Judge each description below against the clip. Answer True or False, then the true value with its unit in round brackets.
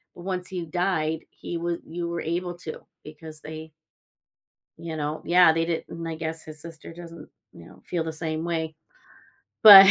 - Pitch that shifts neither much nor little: False (1.5 semitones)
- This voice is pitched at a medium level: True (165 Hz)